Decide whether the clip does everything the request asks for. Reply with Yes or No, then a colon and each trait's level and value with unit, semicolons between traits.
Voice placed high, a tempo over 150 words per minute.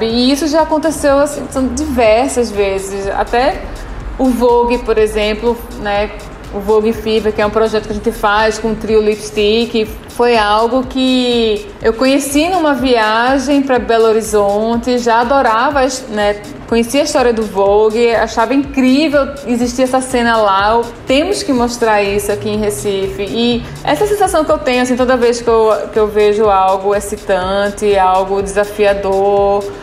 Yes: high, 225 Hz; average, 160 wpm